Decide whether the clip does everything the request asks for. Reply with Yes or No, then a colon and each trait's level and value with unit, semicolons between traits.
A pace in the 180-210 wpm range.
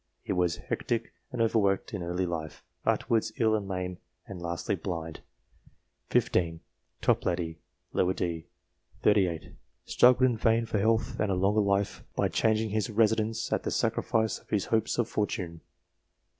No: average, 155 wpm